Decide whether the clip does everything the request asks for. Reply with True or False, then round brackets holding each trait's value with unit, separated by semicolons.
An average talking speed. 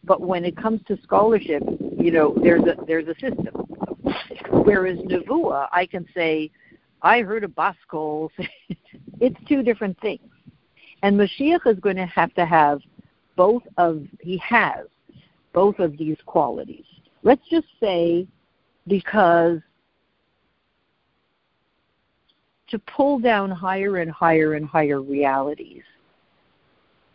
False (120 wpm)